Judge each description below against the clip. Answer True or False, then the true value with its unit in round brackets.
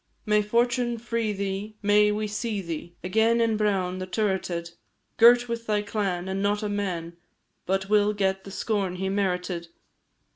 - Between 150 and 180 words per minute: True (160 wpm)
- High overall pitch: True (205 Hz)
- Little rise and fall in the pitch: True (2.3 semitones)